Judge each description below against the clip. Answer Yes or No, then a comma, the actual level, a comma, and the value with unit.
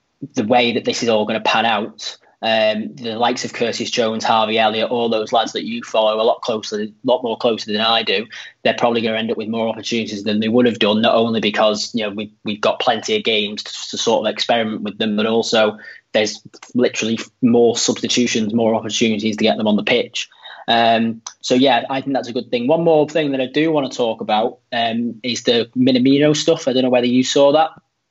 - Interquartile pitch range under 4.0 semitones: Yes, average, 3.0 semitones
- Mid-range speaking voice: No, low, 115 Hz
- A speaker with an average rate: No, fast, 235 wpm